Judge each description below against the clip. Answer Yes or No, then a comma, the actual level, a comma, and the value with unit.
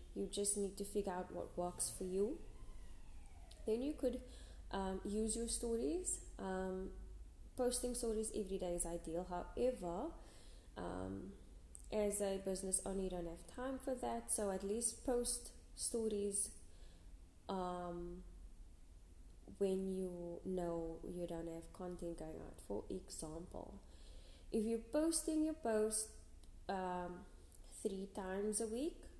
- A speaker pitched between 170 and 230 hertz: Yes, medium, 185 Hz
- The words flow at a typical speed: No, slow, 130 wpm